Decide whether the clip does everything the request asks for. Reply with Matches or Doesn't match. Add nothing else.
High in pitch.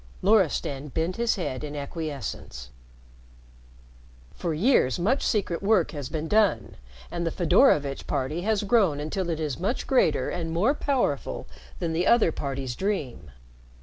Doesn't match